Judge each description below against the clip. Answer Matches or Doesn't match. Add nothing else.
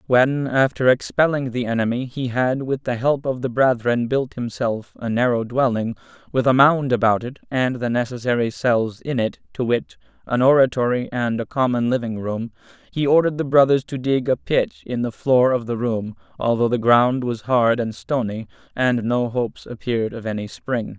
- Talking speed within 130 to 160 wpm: Doesn't match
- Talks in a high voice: Doesn't match